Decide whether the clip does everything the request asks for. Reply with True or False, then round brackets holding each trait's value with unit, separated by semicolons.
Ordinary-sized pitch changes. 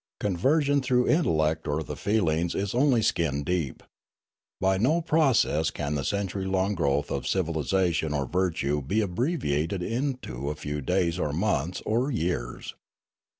False (6.5 semitones)